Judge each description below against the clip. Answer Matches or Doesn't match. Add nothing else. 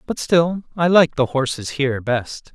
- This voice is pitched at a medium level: Matches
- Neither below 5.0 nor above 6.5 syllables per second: Doesn't match